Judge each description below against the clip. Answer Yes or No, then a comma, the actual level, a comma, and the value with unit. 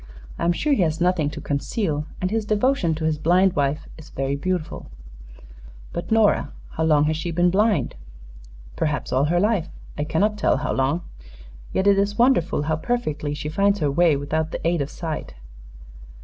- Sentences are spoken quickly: No, average, 185 wpm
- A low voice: No, medium, 165 Hz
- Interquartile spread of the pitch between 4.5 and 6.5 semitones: Yes, average, 4.8 semitones